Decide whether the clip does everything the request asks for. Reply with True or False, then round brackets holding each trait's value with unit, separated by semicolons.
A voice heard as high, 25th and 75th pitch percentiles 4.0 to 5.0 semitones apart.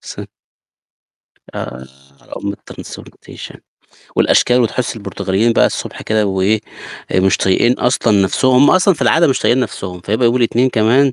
False (115 Hz; 4.3 semitones)